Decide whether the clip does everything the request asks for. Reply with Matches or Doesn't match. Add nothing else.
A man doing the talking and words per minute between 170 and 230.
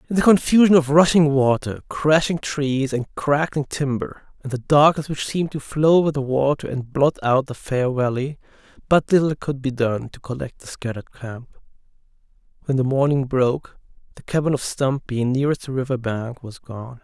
Matches